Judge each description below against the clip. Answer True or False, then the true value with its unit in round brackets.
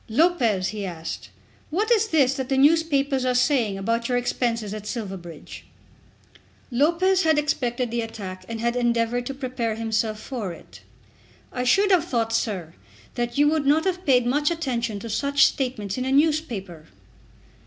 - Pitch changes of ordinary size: True (4.6 semitones)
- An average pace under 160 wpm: False (165 wpm)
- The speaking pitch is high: True (245 Hz)